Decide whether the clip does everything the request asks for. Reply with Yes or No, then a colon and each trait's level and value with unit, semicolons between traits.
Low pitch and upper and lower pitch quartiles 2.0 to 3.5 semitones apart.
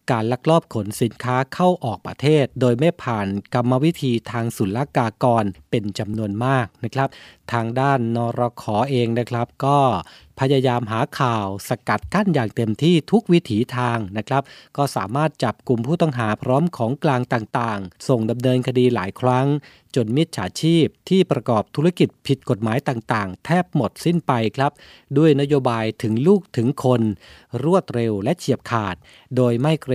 No: low, 125 Hz; average, 4.0 semitones